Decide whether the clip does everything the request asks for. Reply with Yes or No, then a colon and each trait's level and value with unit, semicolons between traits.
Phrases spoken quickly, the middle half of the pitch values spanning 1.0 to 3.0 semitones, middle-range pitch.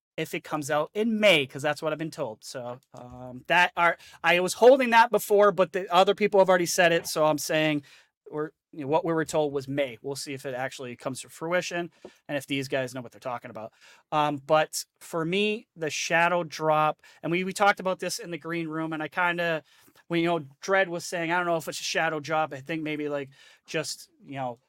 No: fast, 240 wpm; average, 3.4 semitones; medium, 160 Hz